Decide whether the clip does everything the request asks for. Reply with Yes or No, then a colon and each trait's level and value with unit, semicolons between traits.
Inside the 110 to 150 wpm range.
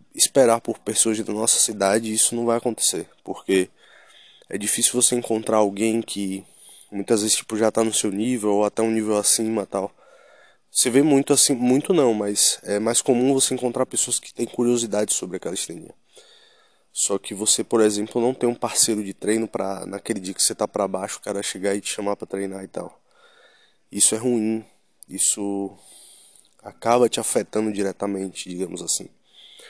No: average, 180 wpm